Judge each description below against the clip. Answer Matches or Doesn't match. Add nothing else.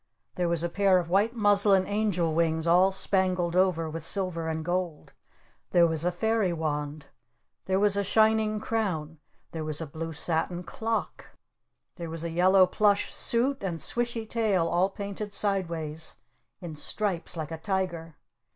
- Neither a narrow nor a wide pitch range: Matches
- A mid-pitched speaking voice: Matches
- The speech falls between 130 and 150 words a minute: Doesn't match